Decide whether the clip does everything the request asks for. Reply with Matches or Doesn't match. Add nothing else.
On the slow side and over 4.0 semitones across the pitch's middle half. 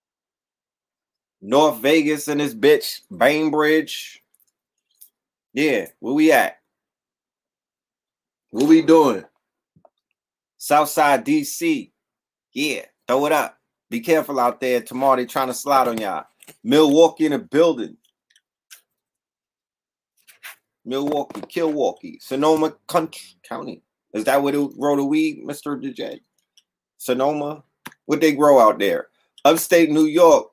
Doesn't match